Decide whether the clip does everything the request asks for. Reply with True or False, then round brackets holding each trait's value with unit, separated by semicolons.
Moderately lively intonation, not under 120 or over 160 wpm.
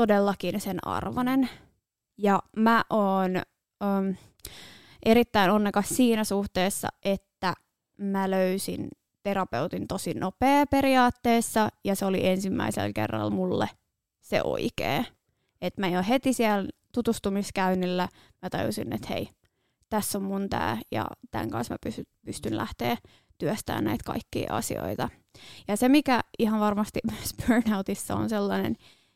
True (3.4 semitones; 125 wpm)